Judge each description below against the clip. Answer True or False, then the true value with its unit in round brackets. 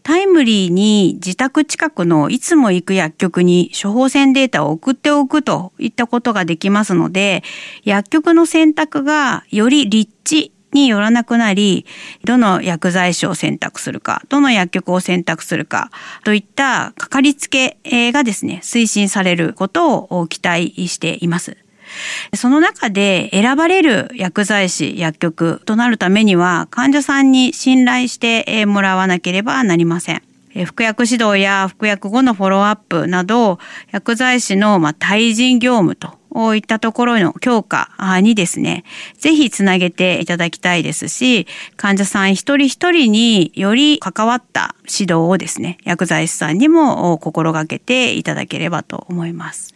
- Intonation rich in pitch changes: True (6.1 semitones)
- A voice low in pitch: False (210 Hz)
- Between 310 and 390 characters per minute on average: False (300 characters per minute)